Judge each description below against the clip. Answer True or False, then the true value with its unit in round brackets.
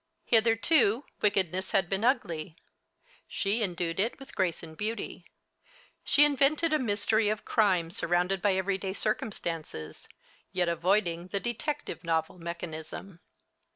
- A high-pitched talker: True (195 Hz)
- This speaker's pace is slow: True (120 wpm)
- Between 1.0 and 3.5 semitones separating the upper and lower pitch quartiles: False (4.6 semitones)